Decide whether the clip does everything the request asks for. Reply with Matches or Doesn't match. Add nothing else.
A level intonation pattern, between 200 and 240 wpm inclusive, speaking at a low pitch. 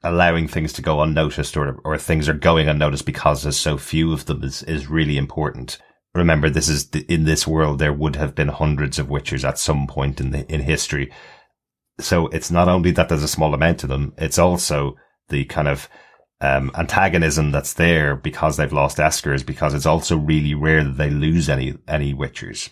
Matches